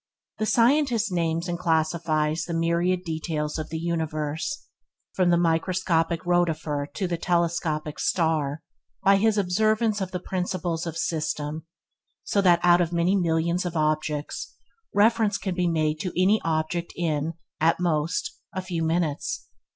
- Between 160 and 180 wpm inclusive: No, average, 150 wpm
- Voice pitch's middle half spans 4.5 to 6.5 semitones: No, narrow, 2.5 semitones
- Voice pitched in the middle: Yes, medium, 170 Hz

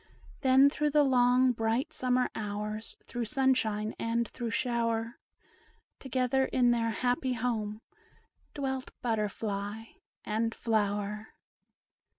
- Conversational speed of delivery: No, slow, 105 wpm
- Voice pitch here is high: Yes, high, 235 Hz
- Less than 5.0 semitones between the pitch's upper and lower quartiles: Yes, average, 2.8 semitones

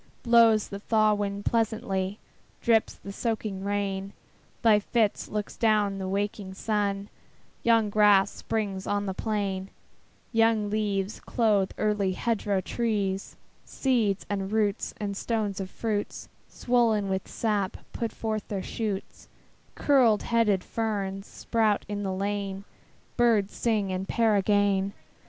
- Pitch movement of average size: No, narrow, 2.1 semitones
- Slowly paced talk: Yes, slow, 130 wpm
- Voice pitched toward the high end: Yes, high, 205 Hz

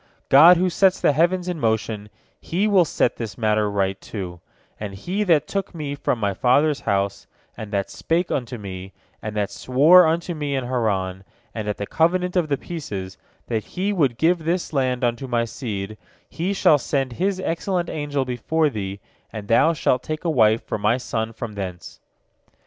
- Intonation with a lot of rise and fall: Yes, wide, 7.7 semitones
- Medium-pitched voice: No, low, 130 Hz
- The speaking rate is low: No, average, 185 wpm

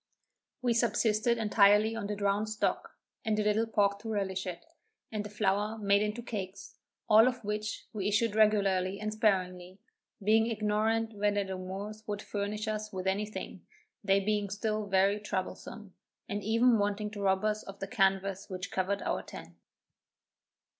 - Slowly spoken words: No, average, 165 wpm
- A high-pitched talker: Yes, high, 210 Hz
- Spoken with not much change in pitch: Yes, narrow, 1.5 semitones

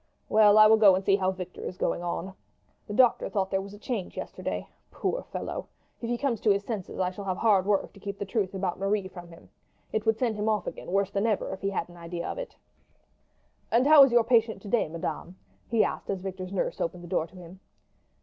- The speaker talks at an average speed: No, fast, 245 wpm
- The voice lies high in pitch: Yes, high, 200 Hz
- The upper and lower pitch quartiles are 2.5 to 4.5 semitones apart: Yes, average, 2.9 semitones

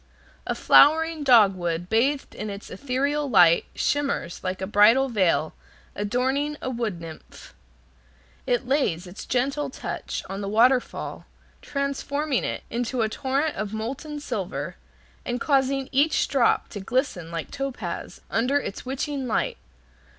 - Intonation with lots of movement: Yes, wide, 5.8 semitones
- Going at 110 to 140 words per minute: Yes, slow, 135 wpm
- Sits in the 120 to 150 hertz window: No, very high, 250 Hz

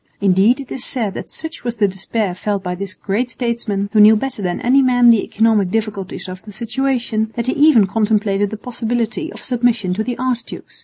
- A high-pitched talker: Yes, high, 220 Hz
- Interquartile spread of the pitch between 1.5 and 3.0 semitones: No, average, 3.4 semitones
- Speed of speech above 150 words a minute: Yes, fast, 205 wpm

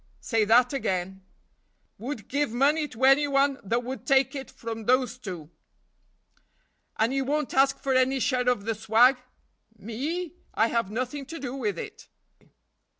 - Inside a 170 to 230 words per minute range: No, average, 155 wpm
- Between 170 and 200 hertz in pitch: No, very high, 255 Hz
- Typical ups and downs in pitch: Yes, average, 3.4 semitones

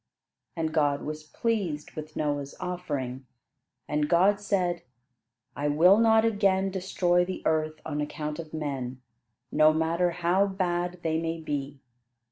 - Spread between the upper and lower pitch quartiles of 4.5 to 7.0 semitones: No, average, 3.3 semitones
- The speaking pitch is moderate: Yes, medium, 165 Hz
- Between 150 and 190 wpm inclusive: No, slow, 135 wpm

